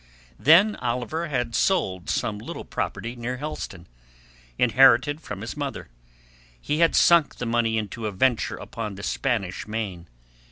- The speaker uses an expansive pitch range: No, average, 5.0 semitones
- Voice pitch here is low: Yes, low, 120 Hz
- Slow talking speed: No, average, 145 wpm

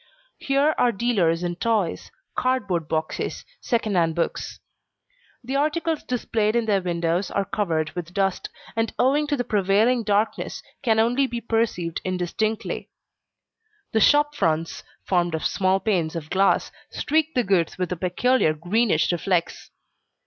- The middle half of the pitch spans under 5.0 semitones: No, wide, 5.6 semitones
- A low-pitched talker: No, high, 200 Hz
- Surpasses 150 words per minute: No, average, 140 wpm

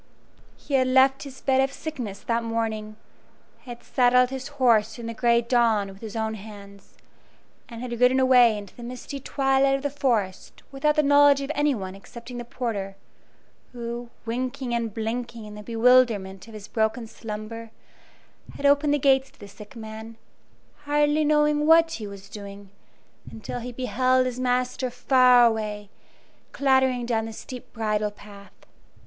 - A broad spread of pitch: No, average, 3.3 semitones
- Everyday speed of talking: Yes, average, 160 wpm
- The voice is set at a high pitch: Yes, high, 240 Hz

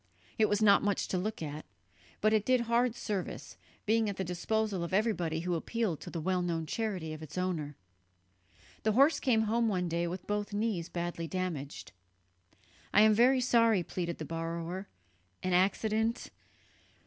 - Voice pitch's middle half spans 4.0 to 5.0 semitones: Yes, average, 4.3 semitones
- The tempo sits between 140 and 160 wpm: No, average, 170 wpm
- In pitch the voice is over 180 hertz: Yes, high, 190 Hz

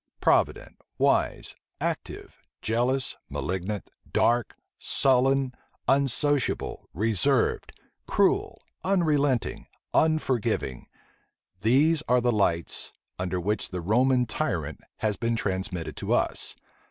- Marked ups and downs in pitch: Yes, wide, 5.7 semitones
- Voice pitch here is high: No, low, 120 Hz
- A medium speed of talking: No, slow, 90 wpm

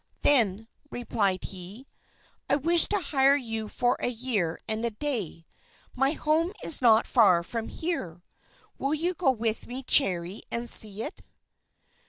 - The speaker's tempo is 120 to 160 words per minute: Yes, average, 150 wpm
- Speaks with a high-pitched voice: Yes, high, 235 Hz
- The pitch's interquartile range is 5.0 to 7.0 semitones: Yes, average, 5.3 semitones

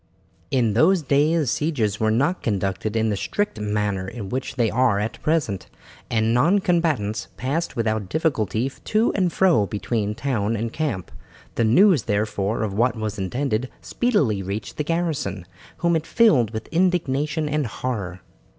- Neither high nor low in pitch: No, low, 120 Hz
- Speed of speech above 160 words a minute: No, average, 155 wpm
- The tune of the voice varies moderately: No, wide, 6.9 semitones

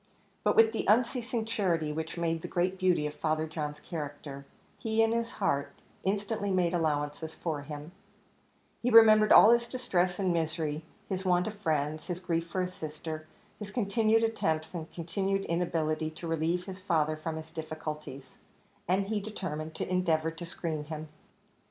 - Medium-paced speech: Yes, average, 165 wpm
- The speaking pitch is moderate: Yes, medium, 170 Hz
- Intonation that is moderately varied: Yes, average, 4.1 semitones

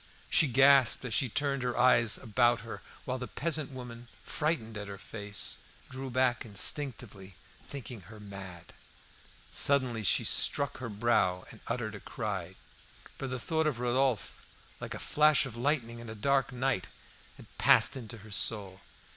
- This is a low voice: Yes, low, 120 Hz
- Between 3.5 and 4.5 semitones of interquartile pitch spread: Yes, average, 4.1 semitones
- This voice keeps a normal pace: Yes, average, 160 wpm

